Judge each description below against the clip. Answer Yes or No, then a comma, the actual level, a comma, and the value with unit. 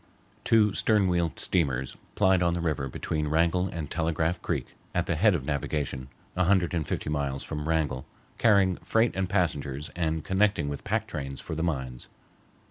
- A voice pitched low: Yes, very low, 80 Hz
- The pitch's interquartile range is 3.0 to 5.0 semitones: Yes, average, 4.3 semitones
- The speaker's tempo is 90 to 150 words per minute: No, average, 175 wpm